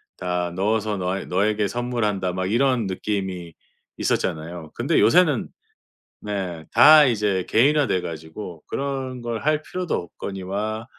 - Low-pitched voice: Yes, low, 105 Hz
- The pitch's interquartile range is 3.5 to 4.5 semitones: No, average, 4.9 semitones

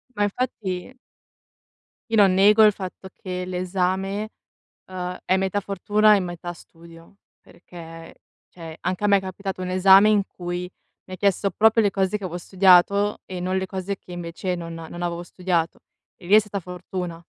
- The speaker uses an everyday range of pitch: No, narrow, 2.1 semitones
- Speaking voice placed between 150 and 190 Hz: Yes, medium, 185 Hz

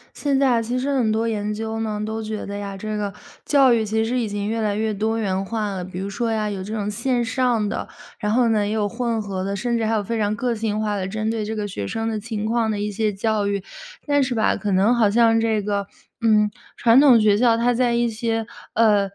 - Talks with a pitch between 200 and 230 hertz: Yes, high, 220 Hz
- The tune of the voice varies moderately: No, narrow, 1.9 semitones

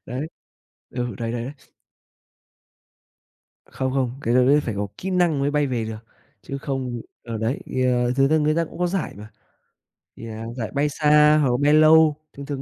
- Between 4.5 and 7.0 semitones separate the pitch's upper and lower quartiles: No, average, 3.8 semitones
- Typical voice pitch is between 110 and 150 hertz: Yes, low, 135 Hz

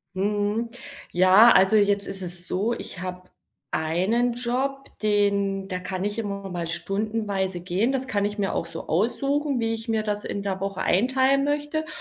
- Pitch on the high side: Yes, high, 205 Hz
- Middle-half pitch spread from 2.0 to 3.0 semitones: No, average, 3.7 semitones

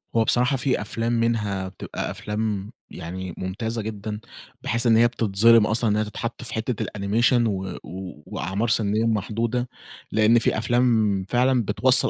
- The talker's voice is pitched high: No, low, 110 Hz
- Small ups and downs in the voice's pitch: Yes, narrow, 2.3 semitones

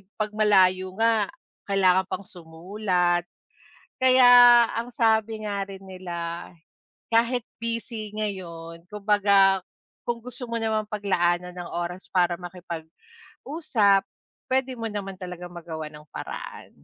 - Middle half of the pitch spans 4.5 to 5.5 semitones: No, average, 3.8 semitones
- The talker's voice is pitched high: Yes, high, 200 Hz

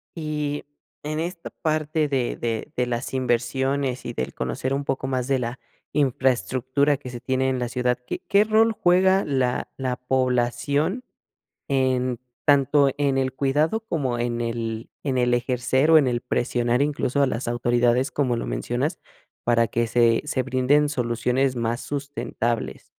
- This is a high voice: No, low, 130 Hz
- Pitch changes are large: No, average, 2.9 semitones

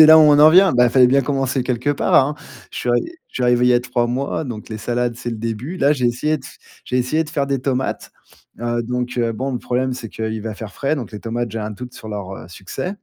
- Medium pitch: No, low, 125 Hz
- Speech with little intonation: No, average, 3.0 semitones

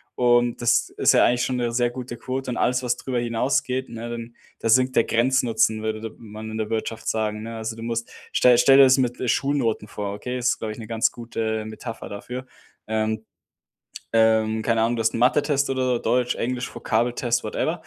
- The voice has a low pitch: Yes, low, 120 Hz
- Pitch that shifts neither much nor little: No, narrow, 2.0 semitones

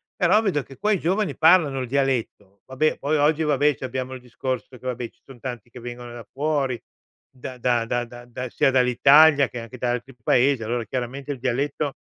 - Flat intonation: No, average, 3.0 semitones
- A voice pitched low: Yes, low, 130 Hz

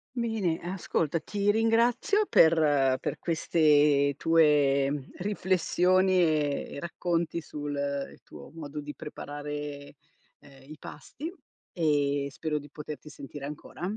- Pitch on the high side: No, medium, 155 Hz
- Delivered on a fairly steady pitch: No, average, 3.5 semitones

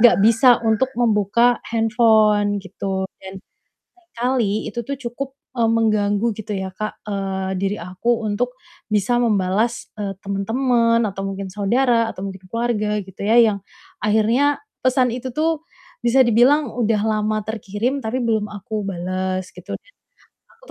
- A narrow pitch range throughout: No, average, 3.2 semitones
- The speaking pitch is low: No, high, 220 Hz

